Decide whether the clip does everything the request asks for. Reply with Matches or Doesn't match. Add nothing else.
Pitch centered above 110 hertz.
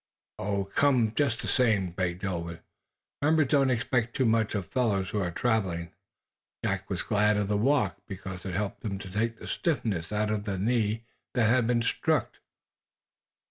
Doesn't match